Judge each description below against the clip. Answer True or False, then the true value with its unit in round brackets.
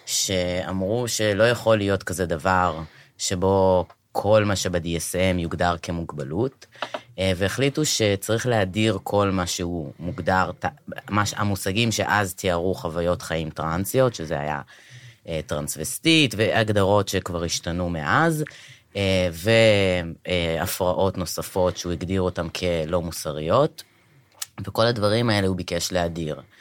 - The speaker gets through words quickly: False (100 wpm)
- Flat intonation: False (3.7 semitones)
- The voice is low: True (95 Hz)